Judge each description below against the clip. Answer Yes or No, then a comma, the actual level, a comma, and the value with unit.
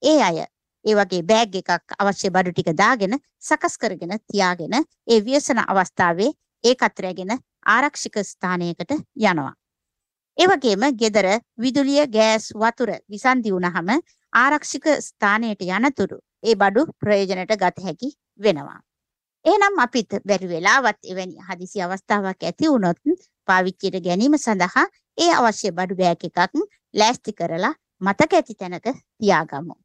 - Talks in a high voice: Yes, high, 210 Hz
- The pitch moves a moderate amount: No, wide, 5.9 semitones